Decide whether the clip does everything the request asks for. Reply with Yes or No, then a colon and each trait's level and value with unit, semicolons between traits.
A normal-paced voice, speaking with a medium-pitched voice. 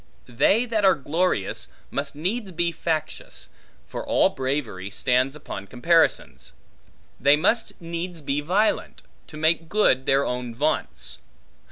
No: slow, 130 wpm; medium, 155 Hz